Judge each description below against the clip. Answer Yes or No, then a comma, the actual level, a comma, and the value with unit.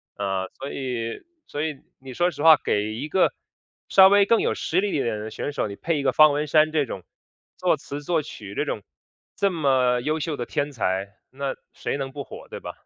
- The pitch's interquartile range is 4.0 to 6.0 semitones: Yes, average, 4.3 semitones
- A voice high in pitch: No, medium, 140 Hz